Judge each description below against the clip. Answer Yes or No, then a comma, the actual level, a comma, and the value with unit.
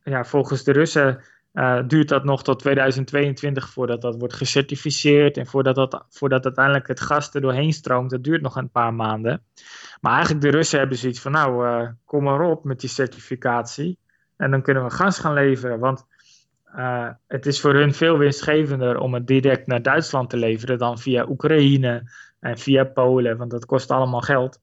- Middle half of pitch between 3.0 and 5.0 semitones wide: No, narrow, 2.4 semitones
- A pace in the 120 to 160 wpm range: No, average, 190 wpm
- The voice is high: No, low, 135 Hz